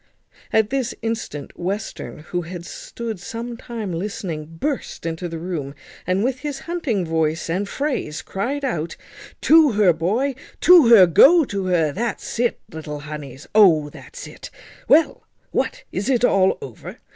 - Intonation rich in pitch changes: Yes, wide, 6.9 semitones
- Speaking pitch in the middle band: No, high, 200 Hz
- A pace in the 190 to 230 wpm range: No, average, 155 wpm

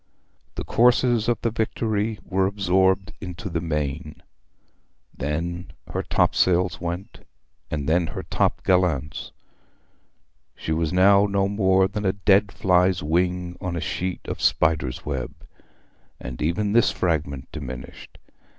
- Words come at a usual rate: No, slow, 130 wpm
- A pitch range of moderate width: Yes, average, 3.6 semitones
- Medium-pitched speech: No, very low, 90 Hz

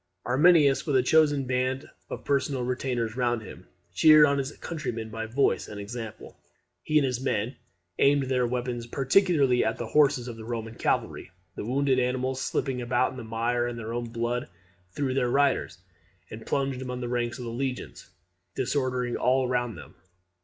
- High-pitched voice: No, low, 125 Hz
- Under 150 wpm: No, average, 175 wpm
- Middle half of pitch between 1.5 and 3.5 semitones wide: Yes, narrow, 2.4 semitones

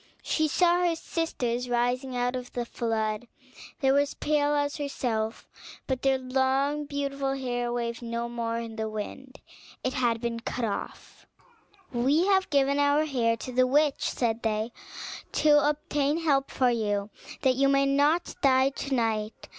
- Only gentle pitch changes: No, average, 3.3 semitones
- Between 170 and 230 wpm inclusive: No, average, 160 wpm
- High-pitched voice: Yes, very high, 260 Hz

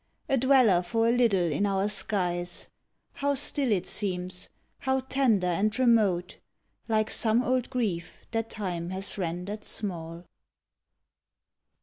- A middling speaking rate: No, slow, 125 wpm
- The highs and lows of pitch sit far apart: No, average, 5.0 semitones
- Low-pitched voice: No, high, 205 Hz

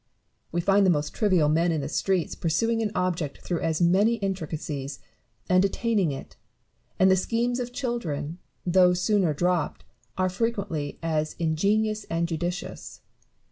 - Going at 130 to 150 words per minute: Yes, average, 145 wpm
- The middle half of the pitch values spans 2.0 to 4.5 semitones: Yes, average, 4.2 semitones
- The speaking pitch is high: No, medium, 180 Hz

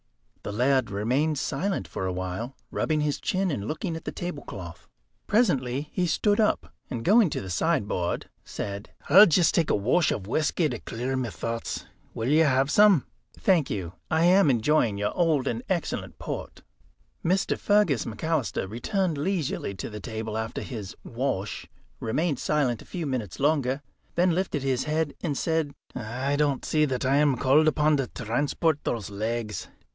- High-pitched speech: No, medium, 140 Hz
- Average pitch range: No, wide, 5.9 semitones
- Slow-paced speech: No, average, 170 wpm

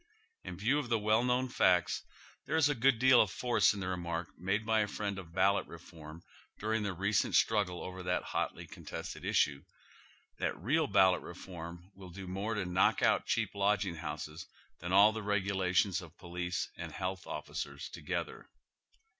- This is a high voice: No, very low, 95 Hz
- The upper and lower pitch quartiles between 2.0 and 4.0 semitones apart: Yes, average, 3.5 semitones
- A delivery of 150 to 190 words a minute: Yes, average, 180 wpm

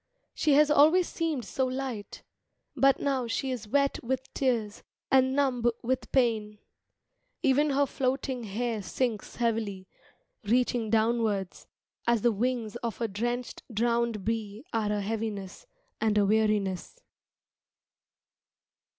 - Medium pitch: No, high, 235 Hz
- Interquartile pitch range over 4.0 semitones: No, average, 3.6 semitones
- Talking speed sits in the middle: No, slow, 125 wpm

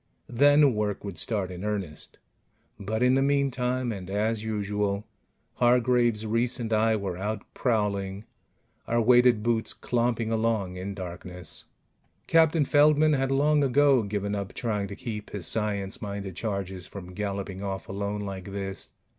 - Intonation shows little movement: No, average, 3.7 semitones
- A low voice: Yes, low, 105 Hz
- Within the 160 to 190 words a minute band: No, average, 145 wpm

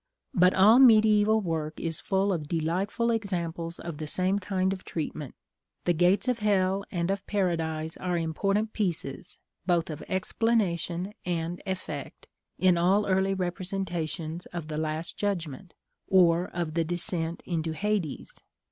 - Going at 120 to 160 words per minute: Yes, average, 140 wpm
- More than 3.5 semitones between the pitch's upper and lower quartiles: No, average, 3.0 semitones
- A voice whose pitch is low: No, medium, 180 Hz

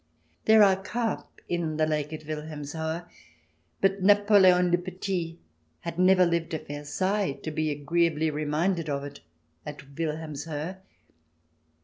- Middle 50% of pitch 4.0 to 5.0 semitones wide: No, average, 3.5 semitones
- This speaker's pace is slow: Yes, slow, 125 wpm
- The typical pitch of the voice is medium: Yes, medium, 165 Hz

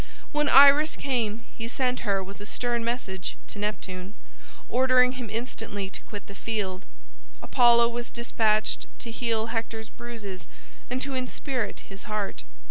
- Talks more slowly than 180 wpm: Yes, average, 145 wpm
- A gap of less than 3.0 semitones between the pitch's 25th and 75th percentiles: No, average, 3.3 semitones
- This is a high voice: Yes, high, 230 Hz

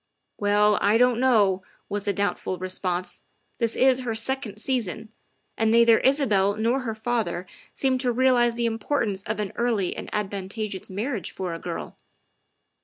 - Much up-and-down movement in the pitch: No, average, 3.3 semitones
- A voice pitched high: Yes, high, 220 Hz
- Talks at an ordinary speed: Yes, average, 175 wpm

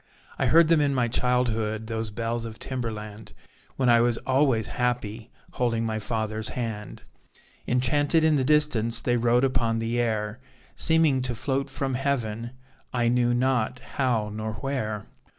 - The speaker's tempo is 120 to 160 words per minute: Yes, average, 150 wpm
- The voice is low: Yes, low, 120 Hz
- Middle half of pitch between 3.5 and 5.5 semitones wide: No, average, 2.9 semitones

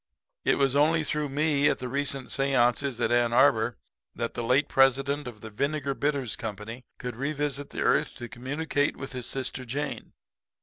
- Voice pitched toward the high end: No, low, 135 Hz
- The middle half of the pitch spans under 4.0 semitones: Yes, average, 3.0 semitones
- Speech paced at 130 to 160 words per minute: No, average, 175 wpm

